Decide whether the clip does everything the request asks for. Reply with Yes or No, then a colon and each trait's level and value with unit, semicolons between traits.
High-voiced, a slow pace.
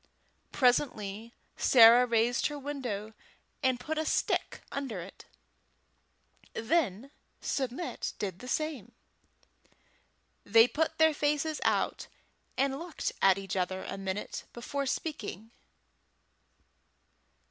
Yes: high, 245 Hz; slow, 105 wpm